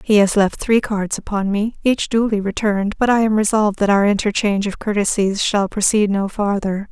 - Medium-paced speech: No, fast, 210 wpm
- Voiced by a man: No, female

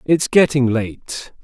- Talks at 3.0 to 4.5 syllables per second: Yes, 3.2 syllables/s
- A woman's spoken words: No, male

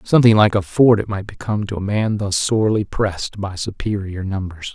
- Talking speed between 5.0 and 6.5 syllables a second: Yes, 5.6 syllables/s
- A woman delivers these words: No, male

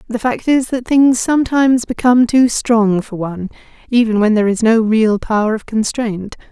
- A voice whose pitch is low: No, high, 230 Hz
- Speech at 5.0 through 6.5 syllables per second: Yes, 5.2 syllables/s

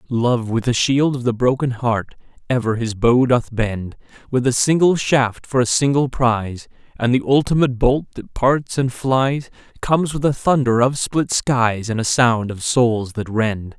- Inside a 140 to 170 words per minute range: No, average, 185 wpm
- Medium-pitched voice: No, low, 125 Hz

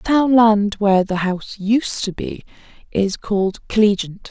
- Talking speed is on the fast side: No, average, 165 wpm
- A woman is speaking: Yes, female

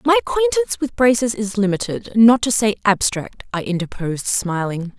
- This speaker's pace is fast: No, average, 155 wpm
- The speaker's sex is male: No, female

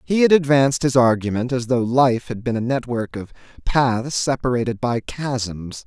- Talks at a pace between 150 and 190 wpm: Yes, average, 175 wpm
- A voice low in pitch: Yes, low, 125 Hz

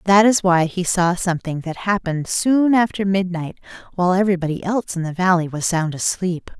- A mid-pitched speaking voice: Yes, medium, 180 Hz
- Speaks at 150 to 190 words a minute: Yes, average, 180 wpm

